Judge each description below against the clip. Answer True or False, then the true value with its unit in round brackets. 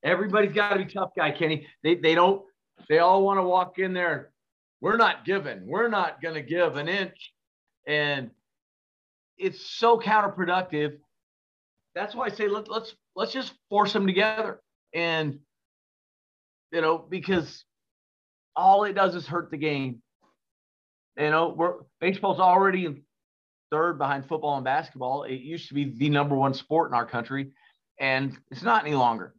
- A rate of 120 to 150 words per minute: False (160 wpm)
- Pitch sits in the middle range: True (160 Hz)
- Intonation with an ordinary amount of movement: False (5.7 semitones)